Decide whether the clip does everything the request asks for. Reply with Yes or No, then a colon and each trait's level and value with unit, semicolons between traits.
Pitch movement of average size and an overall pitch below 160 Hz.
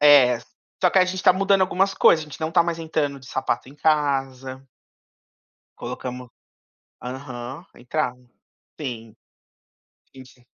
Yes: average, 4.2 semitones; medium, 140 Hz